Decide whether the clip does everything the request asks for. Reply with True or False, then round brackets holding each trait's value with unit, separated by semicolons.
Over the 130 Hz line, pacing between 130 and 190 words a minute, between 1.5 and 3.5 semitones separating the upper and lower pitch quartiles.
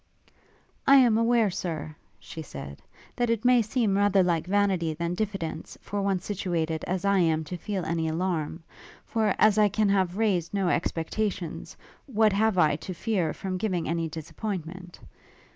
False (185 Hz; 160 wpm; 4.2 semitones)